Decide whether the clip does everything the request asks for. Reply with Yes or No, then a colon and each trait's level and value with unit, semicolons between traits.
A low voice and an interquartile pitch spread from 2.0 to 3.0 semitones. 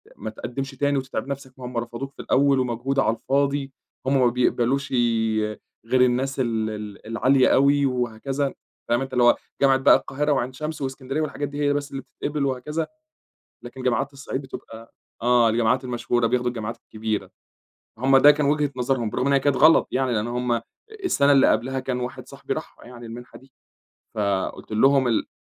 Yes: low, 130 Hz; narrow, 2.5 semitones